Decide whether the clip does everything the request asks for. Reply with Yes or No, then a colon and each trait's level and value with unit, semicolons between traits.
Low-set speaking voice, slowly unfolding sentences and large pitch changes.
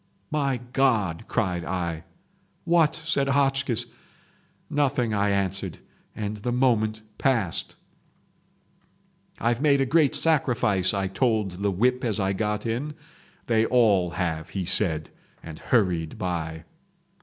Yes: low, 110 Hz; slow, 120 wpm; wide, 5.7 semitones